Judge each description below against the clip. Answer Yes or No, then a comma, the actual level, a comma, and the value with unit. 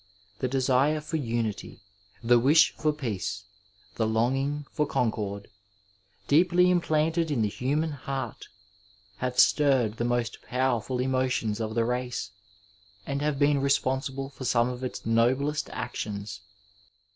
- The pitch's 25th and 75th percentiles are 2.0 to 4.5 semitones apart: Yes, average, 3.8 semitones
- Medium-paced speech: No, slow, 130 wpm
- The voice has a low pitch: Yes, low, 130 Hz